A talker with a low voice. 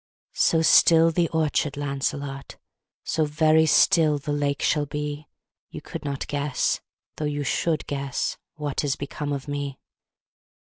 No: medium, 145 Hz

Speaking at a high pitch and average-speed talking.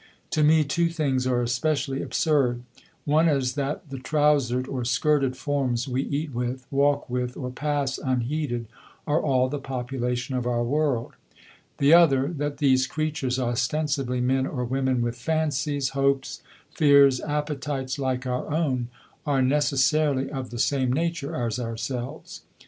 No: low, 135 Hz; average, 145 wpm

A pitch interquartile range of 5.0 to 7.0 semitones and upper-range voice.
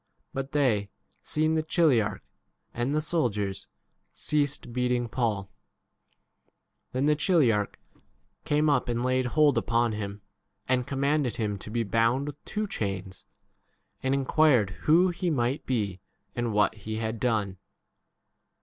No: wide, 5.5 semitones; low, 125 Hz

